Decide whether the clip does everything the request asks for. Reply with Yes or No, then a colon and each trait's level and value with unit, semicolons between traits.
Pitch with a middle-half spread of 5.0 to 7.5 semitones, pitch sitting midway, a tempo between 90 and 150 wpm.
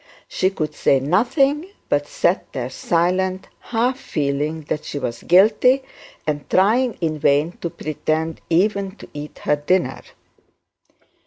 Yes: average, 5.3 semitones; medium, 170 Hz; slow, 135 wpm